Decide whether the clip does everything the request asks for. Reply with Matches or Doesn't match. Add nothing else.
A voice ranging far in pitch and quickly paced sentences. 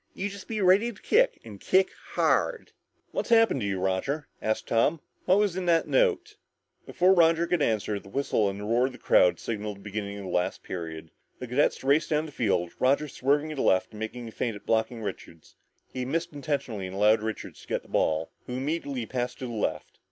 Matches